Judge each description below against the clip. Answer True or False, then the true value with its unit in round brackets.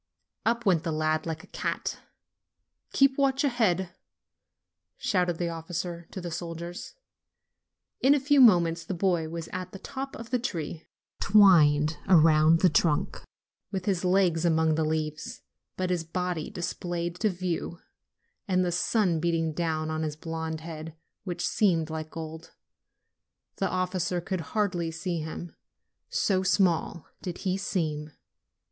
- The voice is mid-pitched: True (170 Hz)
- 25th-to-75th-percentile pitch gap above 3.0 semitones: False (2.6 semitones)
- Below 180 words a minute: True (150 wpm)